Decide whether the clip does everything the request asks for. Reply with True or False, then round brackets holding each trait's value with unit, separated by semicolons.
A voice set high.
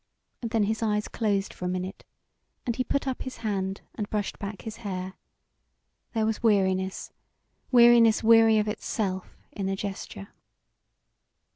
True (210 Hz)